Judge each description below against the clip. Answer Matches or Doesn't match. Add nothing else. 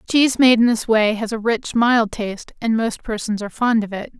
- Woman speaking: Matches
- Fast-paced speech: Matches